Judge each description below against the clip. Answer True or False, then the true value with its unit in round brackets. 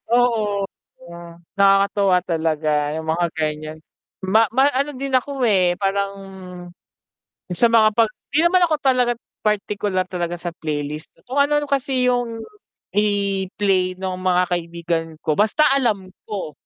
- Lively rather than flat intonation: True (5.7 semitones)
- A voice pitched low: False (200 Hz)